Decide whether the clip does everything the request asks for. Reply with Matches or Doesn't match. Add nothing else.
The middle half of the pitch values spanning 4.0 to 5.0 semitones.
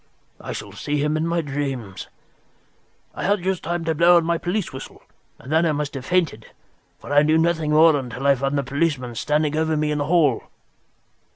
Doesn't match